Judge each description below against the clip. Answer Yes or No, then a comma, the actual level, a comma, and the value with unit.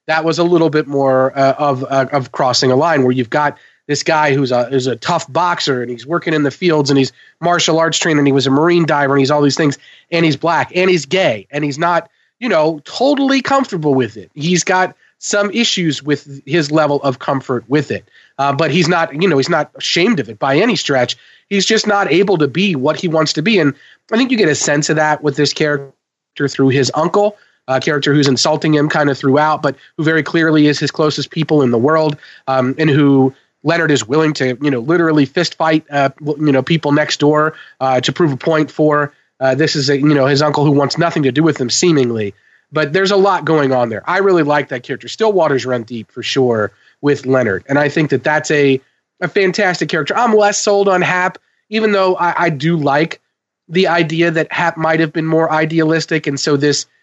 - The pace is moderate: No, fast, 235 wpm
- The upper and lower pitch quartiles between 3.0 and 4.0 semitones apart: Yes, average, 3.4 semitones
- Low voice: No, medium, 150 Hz